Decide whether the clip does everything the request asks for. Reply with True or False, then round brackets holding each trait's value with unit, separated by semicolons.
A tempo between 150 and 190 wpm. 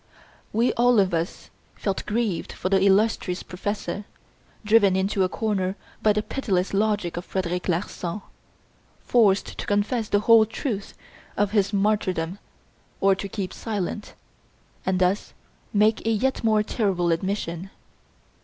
False (135 wpm)